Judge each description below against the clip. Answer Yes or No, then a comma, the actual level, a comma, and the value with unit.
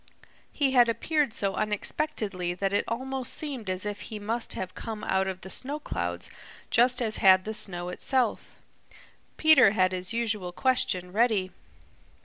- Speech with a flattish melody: No, average, 4.9 semitones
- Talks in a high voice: Yes, high, 215 Hz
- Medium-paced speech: Yes, average, 155 wpm